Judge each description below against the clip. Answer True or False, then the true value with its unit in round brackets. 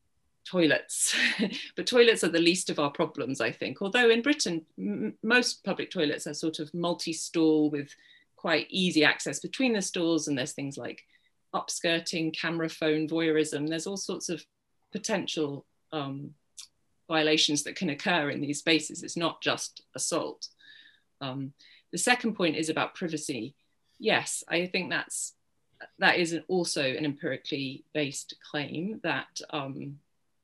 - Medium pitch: True (160 Hz)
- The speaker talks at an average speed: True (150 wpm)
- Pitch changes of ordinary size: True (3.2 semitones)